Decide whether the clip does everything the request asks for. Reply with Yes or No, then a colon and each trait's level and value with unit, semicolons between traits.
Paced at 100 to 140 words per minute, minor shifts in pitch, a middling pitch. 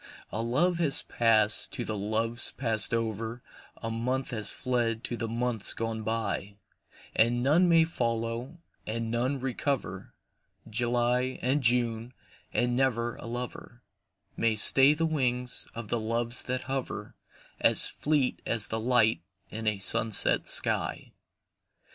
No: slow, 135 wpm; narrow, 2.2 semitones; low, 120 Hz